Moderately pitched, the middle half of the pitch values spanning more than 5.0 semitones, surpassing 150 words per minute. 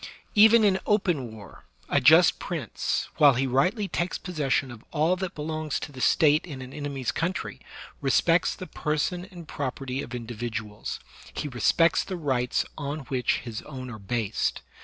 Yes: medium, 145 Hz; wide, 5.4 semitones; average, 160 wpm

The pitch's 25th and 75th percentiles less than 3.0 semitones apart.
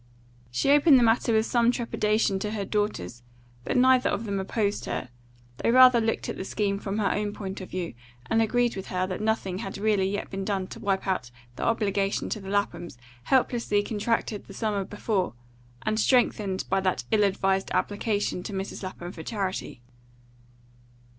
Yes: narrow, 2.6 semitones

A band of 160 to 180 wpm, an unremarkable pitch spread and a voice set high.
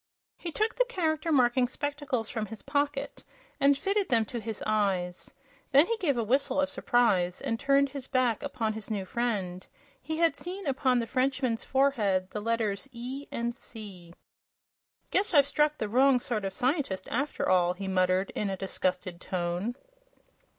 No: average, 170 wpm; wide, 5.8 semitones; high, 240 Hz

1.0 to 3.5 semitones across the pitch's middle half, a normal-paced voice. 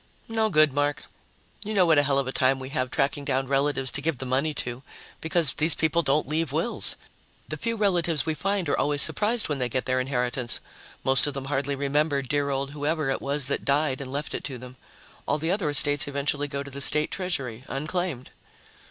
No: average, 2.7 semitones; fast, 220 wpm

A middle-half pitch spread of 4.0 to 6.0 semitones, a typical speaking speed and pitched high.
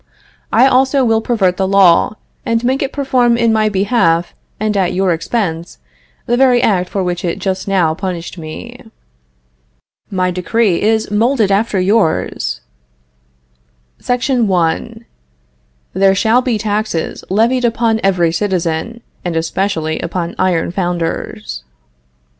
No: average, 4.5 semitones; slow, 130 wpm; high, 195 Hz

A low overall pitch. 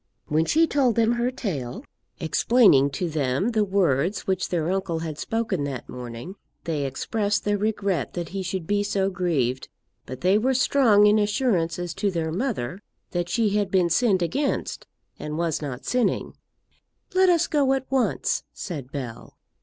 No: high, 190 Hz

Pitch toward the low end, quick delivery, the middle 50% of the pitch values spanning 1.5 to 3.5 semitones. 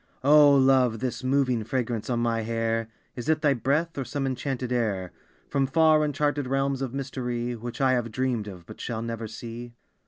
No: low, 125 Hz; average, 185 wpm; average, 2.9 semitones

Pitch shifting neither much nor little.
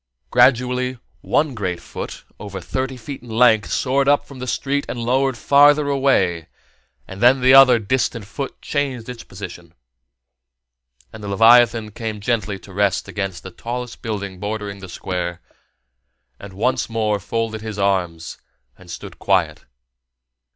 Yes: average, 4.3 semitones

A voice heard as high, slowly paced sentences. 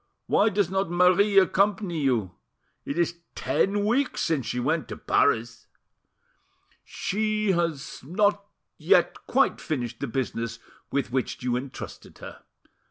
No: medium, 170 Hz; slow, 130 wpm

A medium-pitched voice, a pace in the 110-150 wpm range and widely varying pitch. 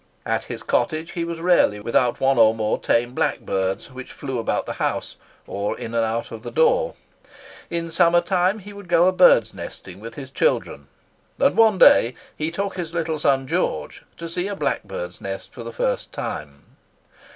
No: medium, 160 Hz; average, 185 wpm; wide, 7.6 semitones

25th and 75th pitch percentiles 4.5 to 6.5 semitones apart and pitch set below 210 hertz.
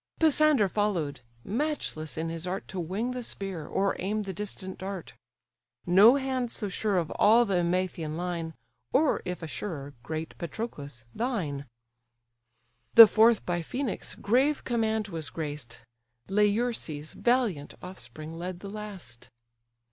Yes: wide, 5.4 semitones; high, 190 Hz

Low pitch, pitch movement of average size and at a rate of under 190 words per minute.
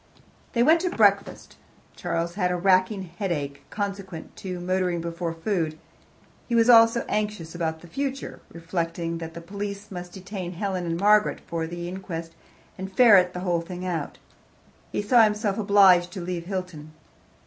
No: medium, 185 Hz; average, 3.2 semitones; average, 160 wpm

